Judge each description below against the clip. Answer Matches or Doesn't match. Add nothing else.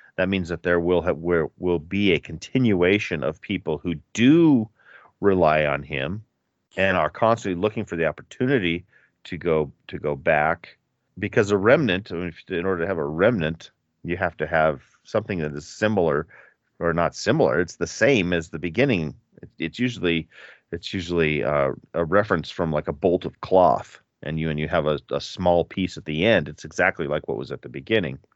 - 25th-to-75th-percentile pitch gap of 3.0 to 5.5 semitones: Matches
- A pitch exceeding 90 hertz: Doesn't match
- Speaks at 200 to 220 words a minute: Doesn't match